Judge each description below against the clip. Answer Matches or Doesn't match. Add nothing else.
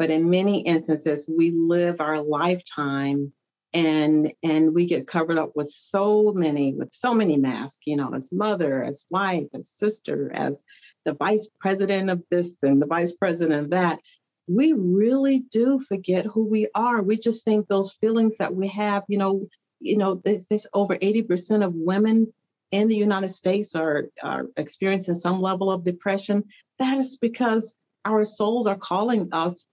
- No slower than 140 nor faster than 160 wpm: Doesn't match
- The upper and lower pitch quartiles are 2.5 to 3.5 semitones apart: Doesn't match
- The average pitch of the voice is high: Matches